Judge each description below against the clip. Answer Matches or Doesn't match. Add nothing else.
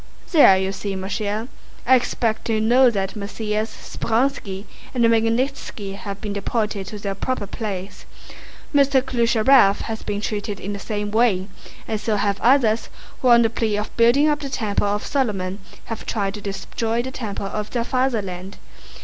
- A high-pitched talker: Matches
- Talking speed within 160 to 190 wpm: Matches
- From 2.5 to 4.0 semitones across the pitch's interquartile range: Matches